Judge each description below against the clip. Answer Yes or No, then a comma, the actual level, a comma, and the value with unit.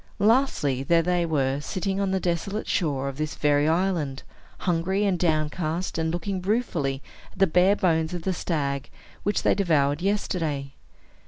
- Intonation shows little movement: No, average, 4.4 semitones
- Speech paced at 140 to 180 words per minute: Yes, average, 160 wpm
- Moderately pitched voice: Yes, medium, 170 Hz